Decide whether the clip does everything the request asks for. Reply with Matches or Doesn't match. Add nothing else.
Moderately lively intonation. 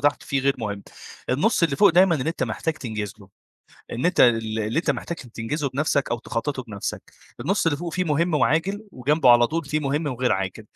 Doesn't match